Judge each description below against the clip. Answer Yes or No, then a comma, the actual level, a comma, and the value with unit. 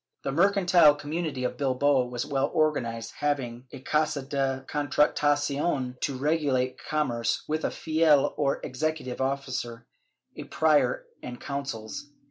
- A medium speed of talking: No, slow, 130 wpm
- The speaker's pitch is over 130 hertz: Yes, medium, 140 Hz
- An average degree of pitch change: Yes, average, 3.0 semitones